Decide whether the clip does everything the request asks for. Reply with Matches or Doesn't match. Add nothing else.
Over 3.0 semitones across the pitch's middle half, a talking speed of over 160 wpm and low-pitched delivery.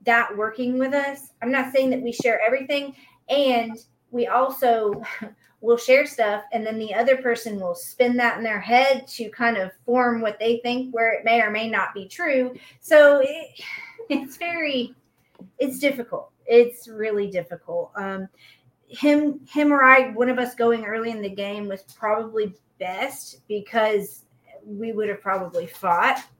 Doesn't match